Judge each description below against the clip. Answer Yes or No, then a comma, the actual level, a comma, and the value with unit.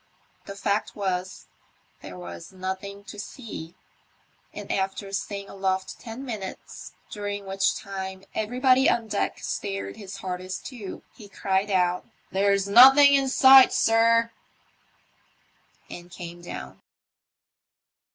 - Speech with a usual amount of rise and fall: Yes, average, 3.1 semitones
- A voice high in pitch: Yes, high, 200 Hz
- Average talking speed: No, slow, 120 wpm